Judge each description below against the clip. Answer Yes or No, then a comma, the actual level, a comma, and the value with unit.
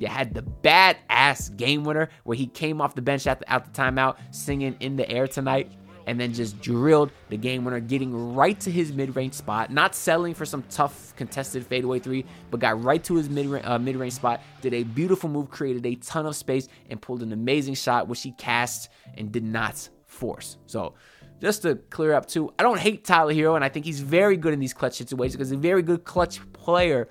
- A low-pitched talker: Yes, low, 130 Hz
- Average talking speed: No, fast, 230 wpm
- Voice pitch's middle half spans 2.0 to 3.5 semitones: No, average, 3.9 semitones